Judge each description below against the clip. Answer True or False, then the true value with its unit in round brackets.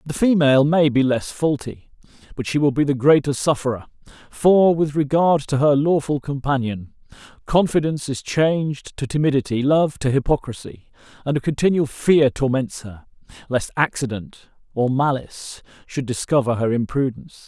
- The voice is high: False (140 Hz)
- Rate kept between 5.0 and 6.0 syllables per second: True (5.1 syllables/s)